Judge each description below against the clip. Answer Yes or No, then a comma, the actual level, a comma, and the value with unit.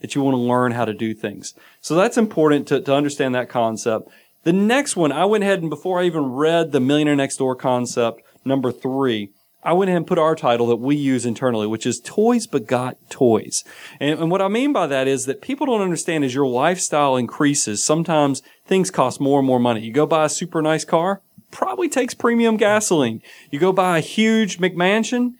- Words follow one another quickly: Yes, fast, 215 wpm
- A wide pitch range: Yes, wide, 6.2 semitones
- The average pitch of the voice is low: No, medium, 150 Hz